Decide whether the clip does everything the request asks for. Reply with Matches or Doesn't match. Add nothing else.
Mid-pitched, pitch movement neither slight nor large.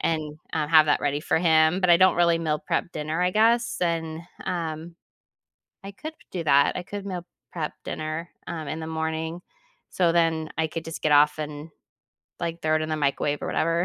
Doesn't match